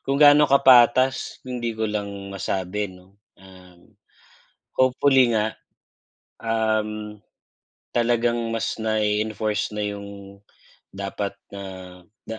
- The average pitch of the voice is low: Yes, low, 110 Hz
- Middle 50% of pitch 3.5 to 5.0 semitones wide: No, average, 2.8 semitones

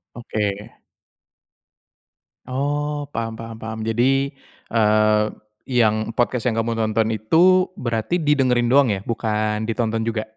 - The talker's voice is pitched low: Yes, low, 115 Hz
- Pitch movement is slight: No, average, 3.0 semitones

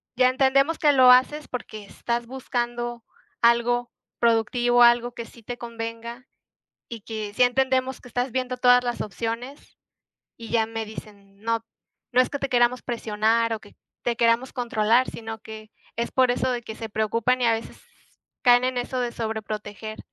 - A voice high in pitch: Yes, high, 235 Hz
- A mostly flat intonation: Yes, narrow, 1.9 semitones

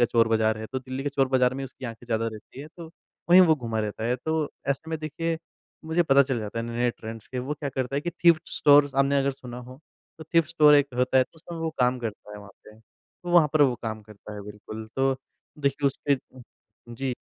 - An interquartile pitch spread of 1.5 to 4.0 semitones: No, average, 4.4 semitones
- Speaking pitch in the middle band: No, low, 130 Hz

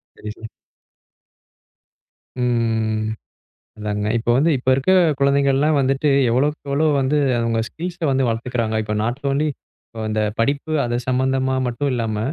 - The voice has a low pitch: Yes, low, 125 Hz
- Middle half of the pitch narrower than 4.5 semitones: Yes, average, 3.5 semitones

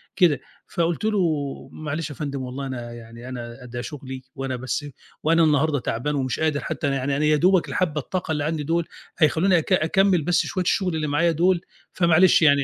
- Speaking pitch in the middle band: Yes, medium, 150 Hz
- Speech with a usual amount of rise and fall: Yes, average, 3.9 semitones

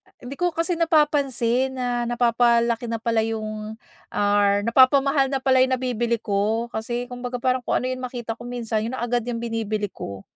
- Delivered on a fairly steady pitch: Yes, narrow, 2.3 semitones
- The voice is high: Yes, high, 240 Hz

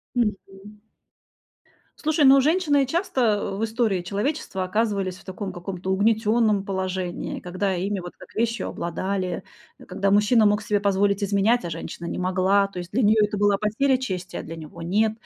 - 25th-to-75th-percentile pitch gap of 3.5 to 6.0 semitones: No, average, 3.0 semitones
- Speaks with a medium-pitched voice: No, high, 200 Hz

